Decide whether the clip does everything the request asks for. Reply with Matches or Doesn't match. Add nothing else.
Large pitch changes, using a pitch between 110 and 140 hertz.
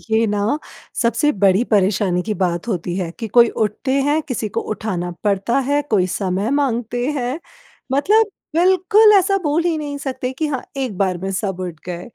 Doesn't match